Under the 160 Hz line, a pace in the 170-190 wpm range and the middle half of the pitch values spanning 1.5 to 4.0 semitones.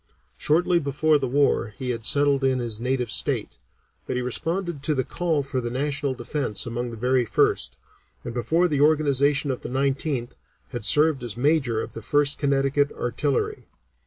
Yes: low, 135 Hz; average, 175 wpm; average, 3.2 semitones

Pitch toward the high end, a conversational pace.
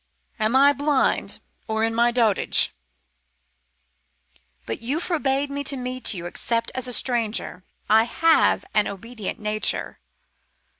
No: high, 240 Hz; slow, 130 wpm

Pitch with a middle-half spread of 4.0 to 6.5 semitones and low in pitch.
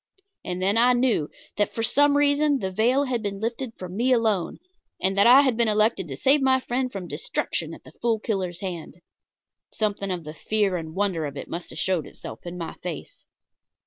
No: wide, 5.4 semitones; high, 210 Hz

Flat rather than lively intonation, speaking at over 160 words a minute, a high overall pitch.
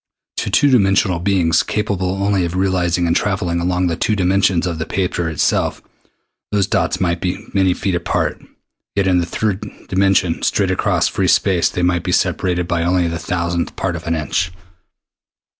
No: narrow, 2.1 semitones; average, 175 wpm; very low, 90 Hz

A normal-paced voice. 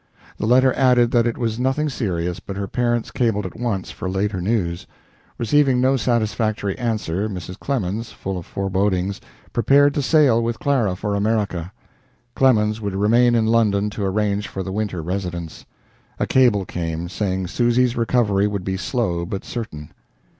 Yes: average, 160 wpm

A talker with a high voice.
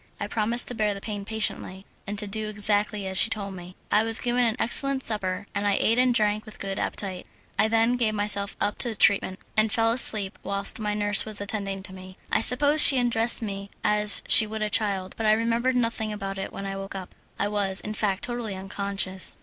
Yes: high, 210 Hz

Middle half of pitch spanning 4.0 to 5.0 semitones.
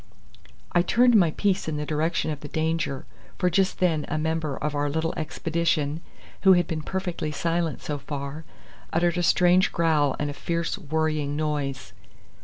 No: average, 2.7 semitones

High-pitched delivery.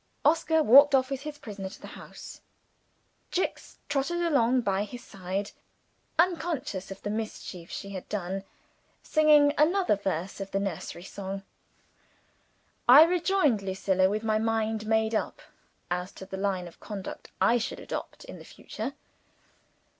Yes: high, 215 Hz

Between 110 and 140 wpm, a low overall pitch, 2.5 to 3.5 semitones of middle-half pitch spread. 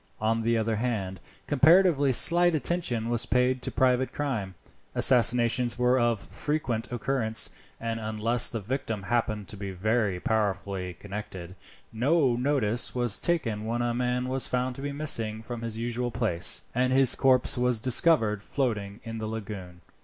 No: average, 155 wpm; low, 120 Hz; average, 3.0 semitones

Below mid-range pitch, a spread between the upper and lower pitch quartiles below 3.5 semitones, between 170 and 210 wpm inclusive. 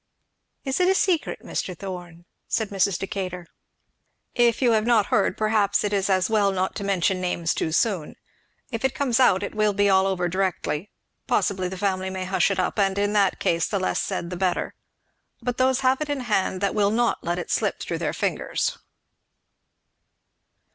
No: high, 195 Hz; average, 3.0 semitones; average, 190 wpm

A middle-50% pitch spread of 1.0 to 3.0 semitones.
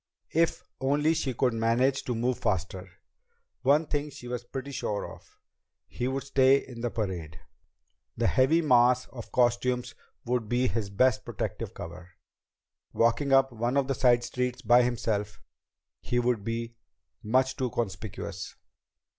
Yes: narrow, 2.5 semitones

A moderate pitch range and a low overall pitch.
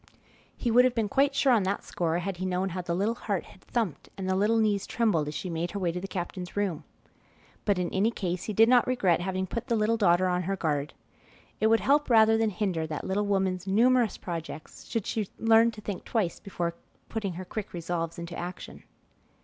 No: average, 4.0 semitones; high, 195 Hz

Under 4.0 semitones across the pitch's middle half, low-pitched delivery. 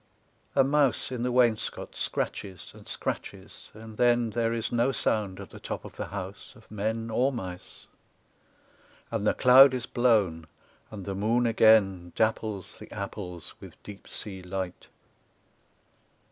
Yes: average, 3.6 semitones; low, 110 Hz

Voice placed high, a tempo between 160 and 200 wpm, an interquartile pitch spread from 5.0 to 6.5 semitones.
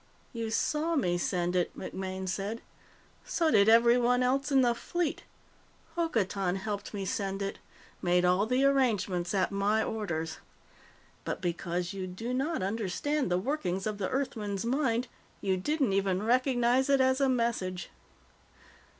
No: high, 215 Hz; average, 145 wpm; wide, 5.4 semitones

